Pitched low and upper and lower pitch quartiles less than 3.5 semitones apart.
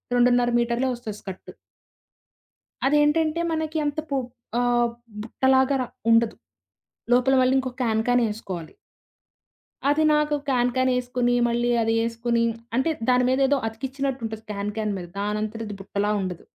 No: high, 245 Hz; average, 3.0 semitones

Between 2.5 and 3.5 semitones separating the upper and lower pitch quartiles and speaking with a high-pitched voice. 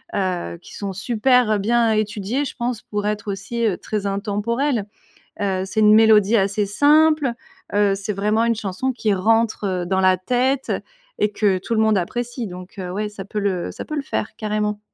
Yes: average, 2.9 semitones; high, 210 Hz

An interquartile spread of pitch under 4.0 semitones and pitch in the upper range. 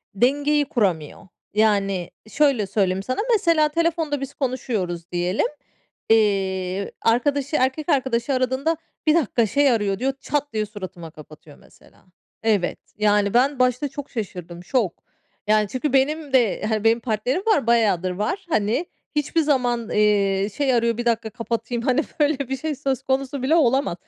No: average, 5.3 semitones; high, 235 Hz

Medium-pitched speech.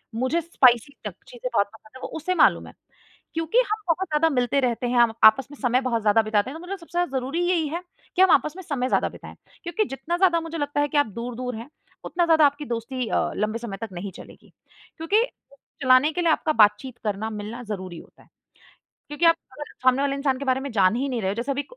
No: very high, 270 Hz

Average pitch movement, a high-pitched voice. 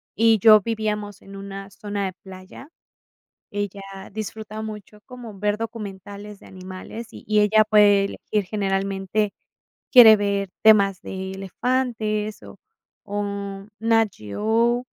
No: narrow, 1.7 semitones; high, 210 Hz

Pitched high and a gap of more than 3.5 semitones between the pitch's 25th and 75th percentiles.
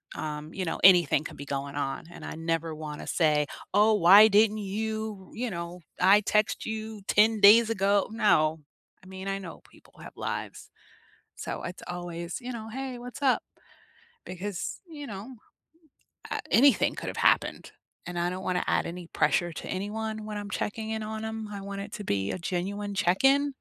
Yes: high, 200 Hz; average, 3.9 semitones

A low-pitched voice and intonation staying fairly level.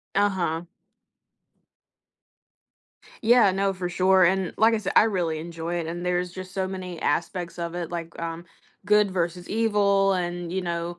No: medium, 180 Hz; narrow, 2.2 semitones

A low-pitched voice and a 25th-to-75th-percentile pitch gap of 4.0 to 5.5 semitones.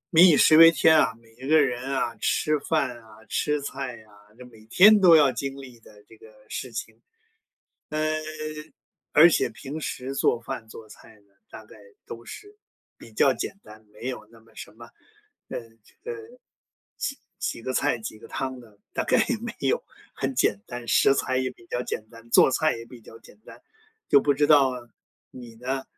Yes: low, 130 Hz; average, 4.5 semitones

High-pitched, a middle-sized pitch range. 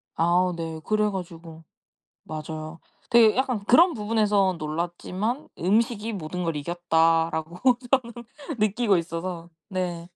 No: medium, 180 Hz; average, 4.3 semitones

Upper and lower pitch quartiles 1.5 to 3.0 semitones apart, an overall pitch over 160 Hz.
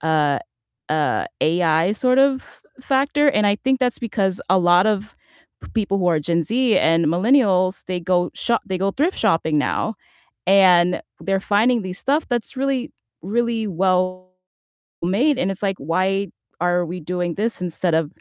No: average, 4.9 semitones; high, 190 Hz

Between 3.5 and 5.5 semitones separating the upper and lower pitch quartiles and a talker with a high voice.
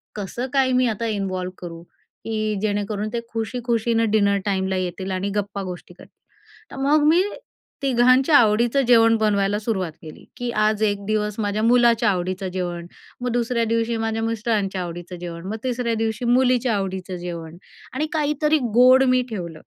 Yes: average, 3.9 semitones; high, 215 Hz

